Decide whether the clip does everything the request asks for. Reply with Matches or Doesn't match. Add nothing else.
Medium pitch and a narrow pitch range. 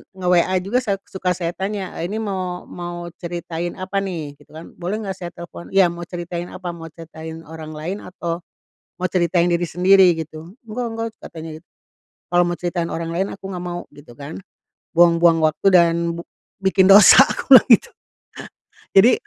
Matches